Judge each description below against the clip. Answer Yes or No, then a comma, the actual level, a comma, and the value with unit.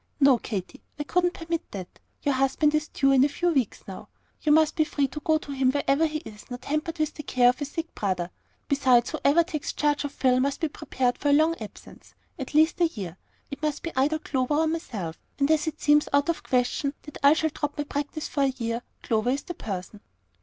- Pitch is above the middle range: Yes, very high, 285 Hz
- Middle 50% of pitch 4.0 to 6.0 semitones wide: No, average, 3.3 semitones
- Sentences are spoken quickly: Yes, fast, 235 wpm